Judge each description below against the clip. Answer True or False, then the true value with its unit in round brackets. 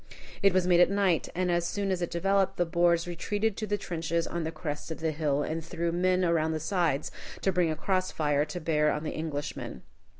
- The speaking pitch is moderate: True (170 Hz)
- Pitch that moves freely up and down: False (2.7 semitones)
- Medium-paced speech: False (230 wpm)